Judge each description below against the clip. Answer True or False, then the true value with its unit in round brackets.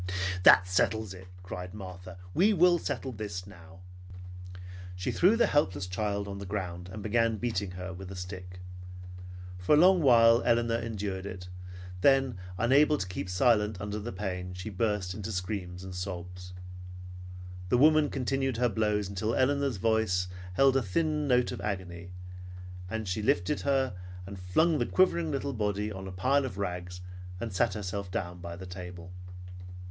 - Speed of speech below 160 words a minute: False (165 wpm)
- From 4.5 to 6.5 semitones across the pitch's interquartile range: True (4.9 semitones)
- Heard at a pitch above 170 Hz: False (100 Hz)